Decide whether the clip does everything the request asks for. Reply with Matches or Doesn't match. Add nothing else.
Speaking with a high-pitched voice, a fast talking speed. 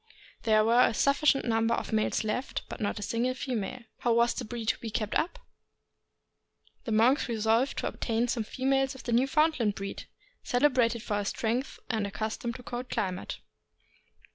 Doesn't match